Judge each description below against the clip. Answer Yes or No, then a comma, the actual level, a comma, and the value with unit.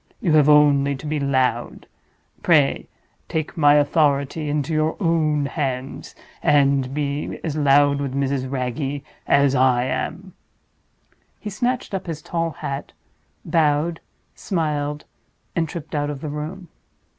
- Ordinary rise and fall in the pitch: No, narrow, 2.3 semitones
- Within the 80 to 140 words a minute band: Yes, slow, 135 wpm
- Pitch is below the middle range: No, medium, 145 Hz